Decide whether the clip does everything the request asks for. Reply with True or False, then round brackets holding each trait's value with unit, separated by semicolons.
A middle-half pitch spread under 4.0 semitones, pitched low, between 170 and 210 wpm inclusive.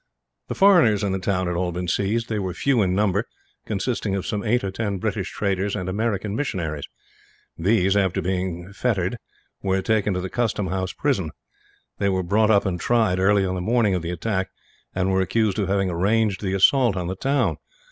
True (2.8 semitones; 95 Hz; 200 wpm)